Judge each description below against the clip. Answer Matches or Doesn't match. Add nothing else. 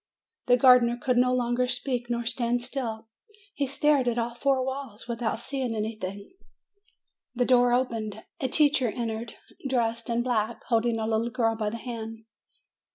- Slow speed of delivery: Doesn't match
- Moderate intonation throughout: Doesn't match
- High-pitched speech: Matches